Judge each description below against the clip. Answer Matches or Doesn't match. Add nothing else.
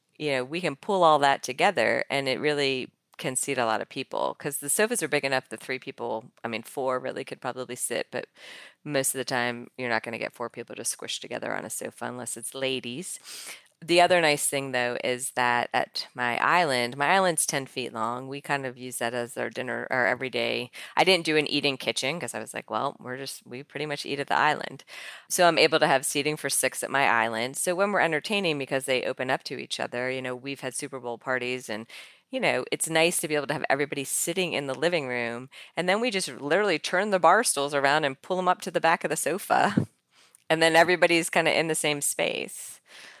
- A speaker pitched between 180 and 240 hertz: Doesn't match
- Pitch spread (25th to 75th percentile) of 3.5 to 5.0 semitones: Matches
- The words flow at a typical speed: Doesn't match